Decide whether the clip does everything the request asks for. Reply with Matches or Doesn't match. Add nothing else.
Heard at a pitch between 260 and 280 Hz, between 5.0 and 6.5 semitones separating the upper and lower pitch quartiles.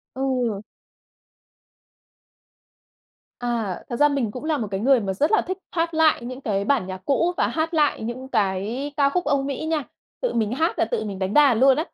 Matches